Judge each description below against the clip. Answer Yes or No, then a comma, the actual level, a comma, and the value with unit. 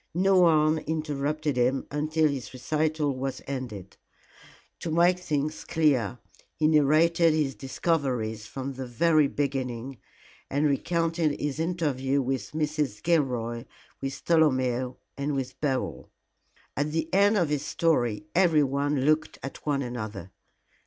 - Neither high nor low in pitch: Yes, medium, 145 Hz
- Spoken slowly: Yes, slow, 125 wpm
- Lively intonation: No, average, 3.3 semitones